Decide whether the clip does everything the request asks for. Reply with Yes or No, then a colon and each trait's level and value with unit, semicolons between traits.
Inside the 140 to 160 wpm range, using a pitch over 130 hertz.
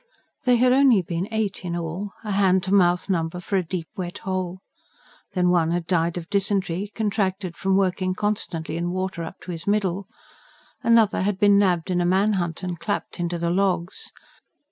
No: average, 185 wpm; medium, 185 Hz